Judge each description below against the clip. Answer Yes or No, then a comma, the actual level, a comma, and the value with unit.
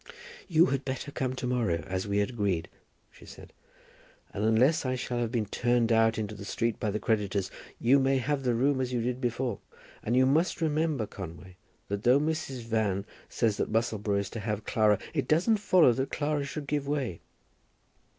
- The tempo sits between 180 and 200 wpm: Yes, average, 195 wpm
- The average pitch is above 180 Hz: No, low, 120 Hz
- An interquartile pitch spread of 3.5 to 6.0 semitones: Yes, average, 4.4 semitones